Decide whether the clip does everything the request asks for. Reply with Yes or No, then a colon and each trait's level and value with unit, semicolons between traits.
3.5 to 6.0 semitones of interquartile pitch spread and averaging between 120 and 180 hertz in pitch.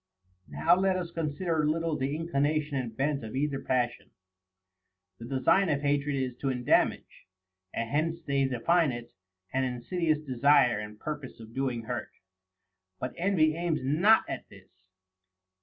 Yes: average, 4.1 semitones; medium, 140 Hz